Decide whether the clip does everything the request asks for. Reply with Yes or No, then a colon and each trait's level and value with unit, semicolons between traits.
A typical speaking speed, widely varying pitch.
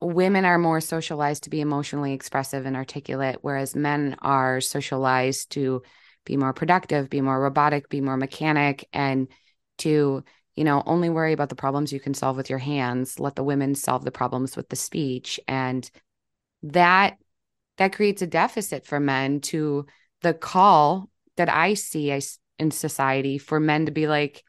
No: average, 170 wpm; narrow, 2.5 semitones